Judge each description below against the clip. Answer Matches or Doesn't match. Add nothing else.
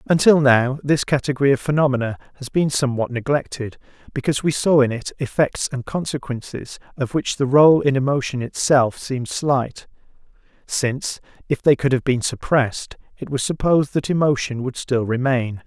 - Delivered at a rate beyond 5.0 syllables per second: Matches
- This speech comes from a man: Matches